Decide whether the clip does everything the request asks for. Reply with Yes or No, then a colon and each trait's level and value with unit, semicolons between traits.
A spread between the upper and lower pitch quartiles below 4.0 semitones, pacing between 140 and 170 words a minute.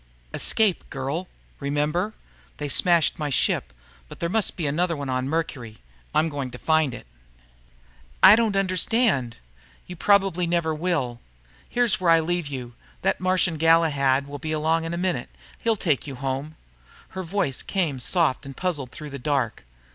No: average, 4.6 semitones; average, 160 wpm